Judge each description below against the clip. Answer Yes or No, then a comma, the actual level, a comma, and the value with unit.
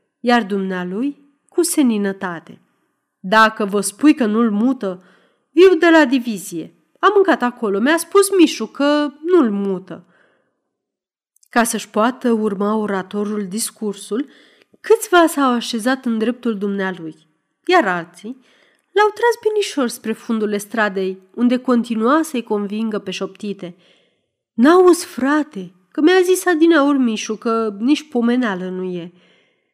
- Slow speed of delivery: No, average, 125 wpm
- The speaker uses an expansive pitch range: Yes, wide, 6.5 semitones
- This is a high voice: Yes, high, 230 Hz